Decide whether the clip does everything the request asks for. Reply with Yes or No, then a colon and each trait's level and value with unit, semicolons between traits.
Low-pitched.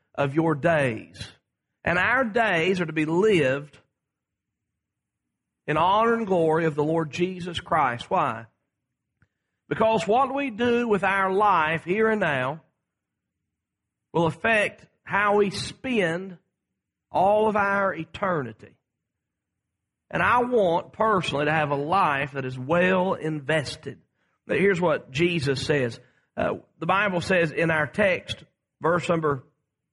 No: medium, 170 Hz